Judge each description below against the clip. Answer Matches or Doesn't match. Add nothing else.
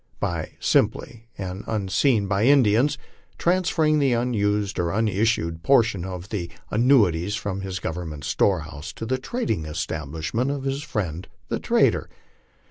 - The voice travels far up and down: Matches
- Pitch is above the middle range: Doesn't match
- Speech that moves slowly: Matches